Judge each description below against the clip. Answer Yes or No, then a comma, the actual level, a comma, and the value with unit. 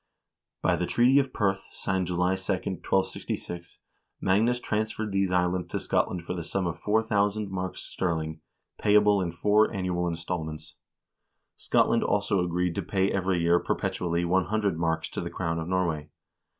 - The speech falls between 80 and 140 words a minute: No, average, 150 wpm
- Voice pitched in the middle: No, very low, 90 Hz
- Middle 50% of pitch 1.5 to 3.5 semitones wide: Yes, average, 2.9 semitones